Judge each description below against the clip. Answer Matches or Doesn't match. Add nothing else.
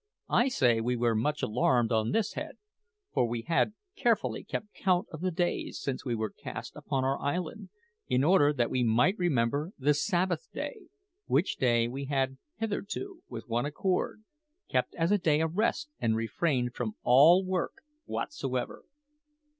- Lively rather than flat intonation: Matches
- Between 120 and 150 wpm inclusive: Doesn't match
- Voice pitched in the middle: Matches